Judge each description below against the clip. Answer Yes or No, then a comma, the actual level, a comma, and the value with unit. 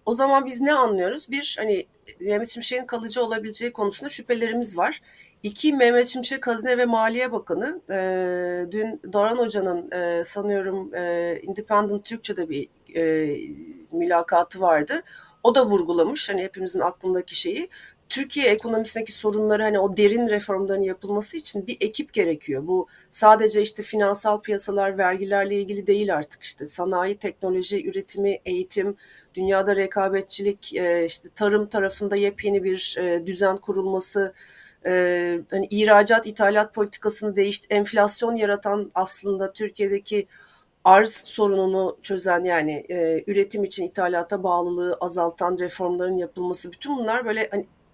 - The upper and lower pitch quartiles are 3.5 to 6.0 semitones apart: No, average, 2.9 semitones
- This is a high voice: Yes, high, 200 Hz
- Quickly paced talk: No, average, 120 wpm